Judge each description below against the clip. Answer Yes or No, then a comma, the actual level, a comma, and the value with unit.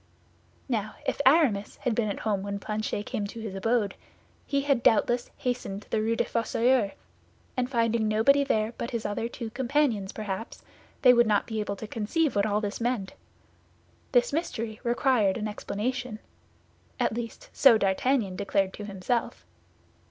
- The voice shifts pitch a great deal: No, average, 3.1 semitones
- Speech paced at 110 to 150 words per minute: No, average, 165 wpm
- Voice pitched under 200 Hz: No, high, 225 Hz